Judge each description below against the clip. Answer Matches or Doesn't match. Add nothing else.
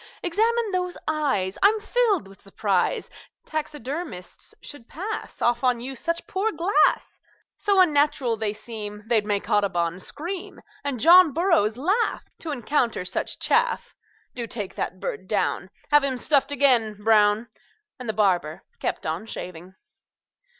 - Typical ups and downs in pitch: Doesn't match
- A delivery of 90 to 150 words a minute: Matches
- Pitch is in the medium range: Doesn't match